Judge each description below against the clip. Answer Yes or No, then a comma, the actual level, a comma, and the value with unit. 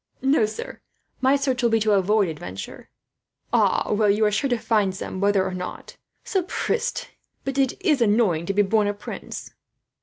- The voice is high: Yes, high, 215 Hz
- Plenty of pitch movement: No, average, 4.5 semitones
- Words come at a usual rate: Yes, average, 180 wpm